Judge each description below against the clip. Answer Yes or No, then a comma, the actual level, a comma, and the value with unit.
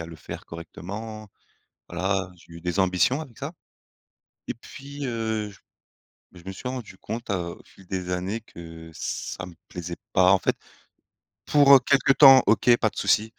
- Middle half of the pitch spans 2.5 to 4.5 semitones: No, average, 5.1 semitones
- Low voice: Yes, low, 100 Hz